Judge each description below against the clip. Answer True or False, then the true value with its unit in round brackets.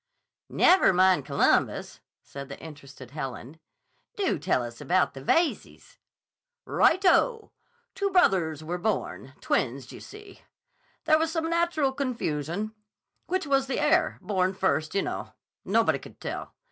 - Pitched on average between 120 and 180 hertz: False (195 Hz)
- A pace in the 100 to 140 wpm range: True (135 wpm)